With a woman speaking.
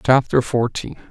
No: male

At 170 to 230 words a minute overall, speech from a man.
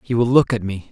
No: fast, 330 wpm; male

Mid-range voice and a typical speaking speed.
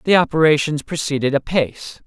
No: medium, 150 Hz; slow, 115 wpm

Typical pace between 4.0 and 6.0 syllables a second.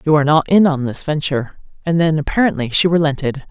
No: 6.6 syllables/s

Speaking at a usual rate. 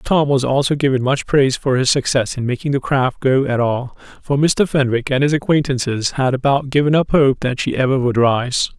No: fast, 220 wpm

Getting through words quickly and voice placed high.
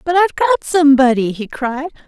No: average, 175 wpm; very high, 285 Hz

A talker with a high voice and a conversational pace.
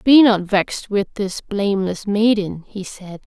Yes: high, 205 Hz; average, 160 wpm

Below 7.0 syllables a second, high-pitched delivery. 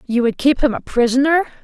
Yes: 5.8 syllables/s; very high, 260 Hz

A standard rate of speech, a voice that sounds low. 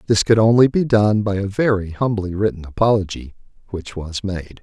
Yes: average, 180 wpm; low, 100 Hz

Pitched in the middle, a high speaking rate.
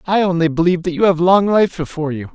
Yes: medium, 175 Hz; fast, 255 wpm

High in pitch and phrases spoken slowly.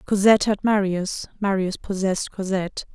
Yes: high, 195 Hz; slow, 120 wpm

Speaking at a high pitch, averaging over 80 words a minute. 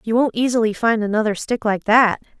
Yes: high, 220 Hz; average, 200 wpm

